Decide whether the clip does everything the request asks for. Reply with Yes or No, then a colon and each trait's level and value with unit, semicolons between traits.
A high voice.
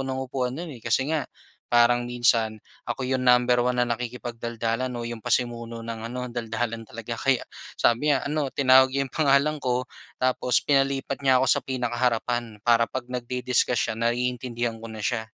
No: low, 125 Hz